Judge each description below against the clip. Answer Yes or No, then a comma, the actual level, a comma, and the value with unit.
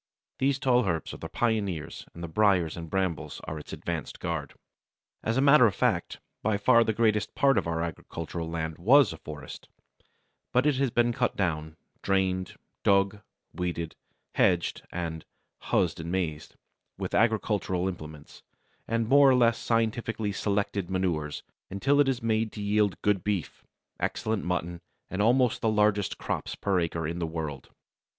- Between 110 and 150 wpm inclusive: No, average, 160 wpm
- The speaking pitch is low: Yes, low, 100 Hz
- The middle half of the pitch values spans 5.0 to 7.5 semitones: Yes, average, 5.3 semitones